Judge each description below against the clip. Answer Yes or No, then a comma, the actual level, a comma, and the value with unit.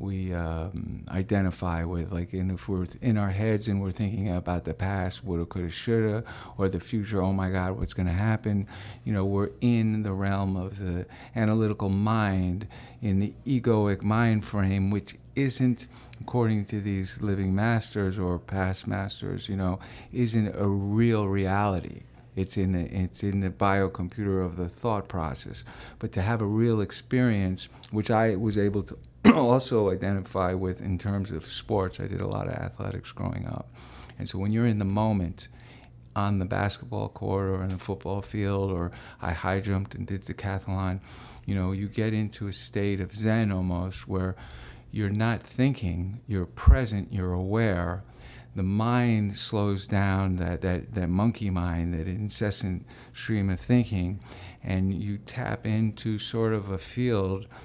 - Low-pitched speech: Yes, low, 100 Hz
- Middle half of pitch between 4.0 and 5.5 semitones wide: No, average, 3.0 semitones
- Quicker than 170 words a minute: No, average, 165 wpm